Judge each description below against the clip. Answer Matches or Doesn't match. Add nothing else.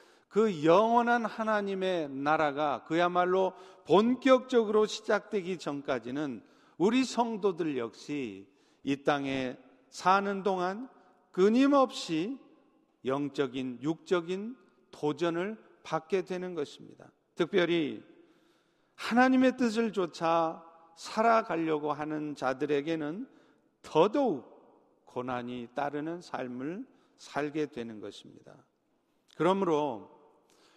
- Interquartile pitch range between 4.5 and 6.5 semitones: Doesn't match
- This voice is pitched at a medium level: Matches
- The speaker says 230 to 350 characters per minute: Doesn't match